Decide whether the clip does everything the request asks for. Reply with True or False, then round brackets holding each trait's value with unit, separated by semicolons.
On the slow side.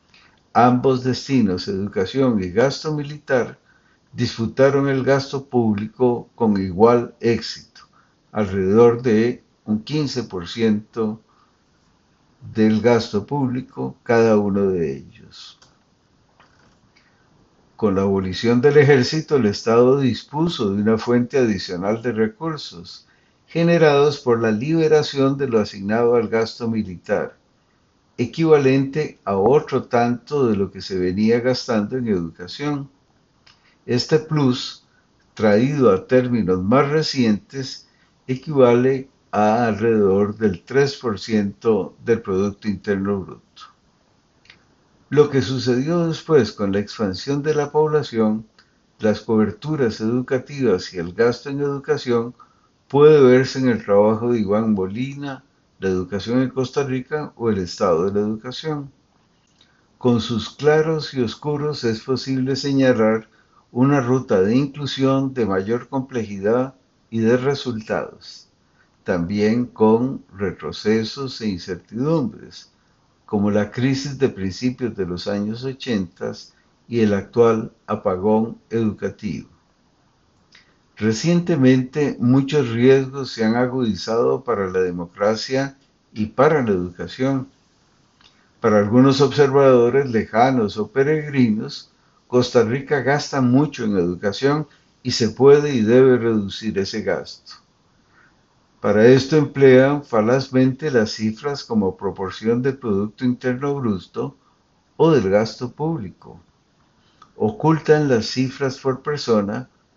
True (110 wpm)